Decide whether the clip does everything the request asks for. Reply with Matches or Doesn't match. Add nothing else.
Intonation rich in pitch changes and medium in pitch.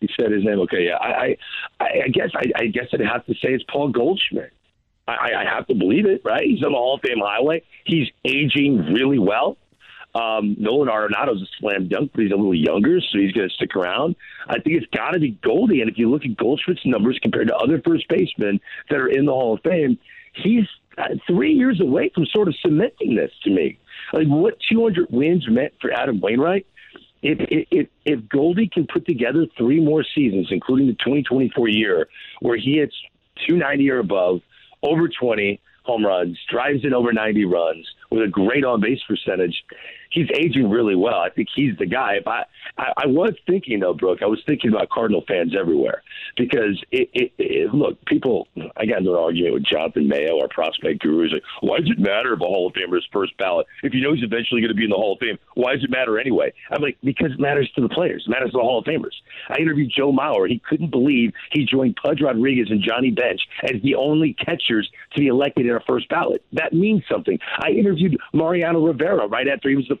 Matches